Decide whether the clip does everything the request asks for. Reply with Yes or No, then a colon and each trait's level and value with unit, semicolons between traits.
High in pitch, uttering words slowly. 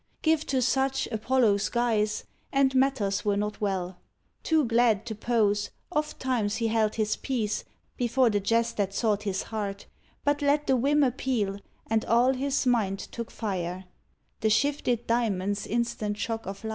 No: high, 225 Hz; average, 160 wpm